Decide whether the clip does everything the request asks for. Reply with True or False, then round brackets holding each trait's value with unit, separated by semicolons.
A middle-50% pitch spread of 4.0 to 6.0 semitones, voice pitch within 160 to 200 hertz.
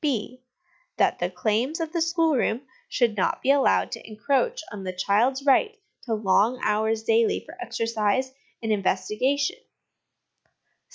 False (5.3 semitones; 240 Hz)